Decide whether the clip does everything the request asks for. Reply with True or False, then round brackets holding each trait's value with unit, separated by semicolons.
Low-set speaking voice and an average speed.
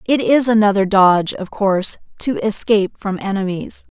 False (205 Hz; 150 wpm)